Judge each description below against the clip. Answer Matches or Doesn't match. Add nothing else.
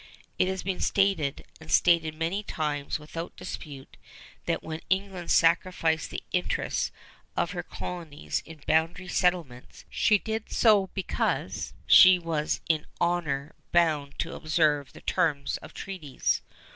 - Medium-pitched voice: Matches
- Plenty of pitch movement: Doesn't match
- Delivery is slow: Matches